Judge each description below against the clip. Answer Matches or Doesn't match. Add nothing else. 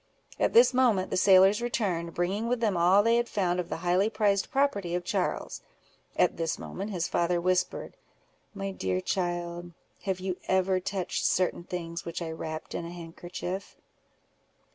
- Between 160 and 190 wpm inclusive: Matches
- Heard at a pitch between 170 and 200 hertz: Matches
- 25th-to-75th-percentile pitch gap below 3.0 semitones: Matches